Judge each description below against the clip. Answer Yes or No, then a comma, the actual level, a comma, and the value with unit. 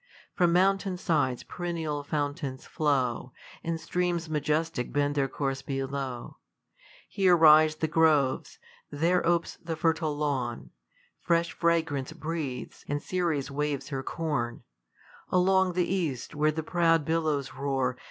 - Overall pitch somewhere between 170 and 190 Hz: No, medium, 155 Hz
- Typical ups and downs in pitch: Yes, average, 3.3 semitones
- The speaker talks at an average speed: No, slow, 125 wpm